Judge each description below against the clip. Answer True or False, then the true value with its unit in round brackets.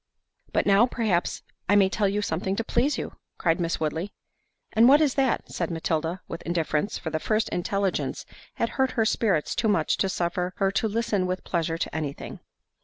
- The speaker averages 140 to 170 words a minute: False (190 wpm)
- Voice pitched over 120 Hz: True (190 Hz)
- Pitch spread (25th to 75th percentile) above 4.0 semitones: True (4.6 semitones)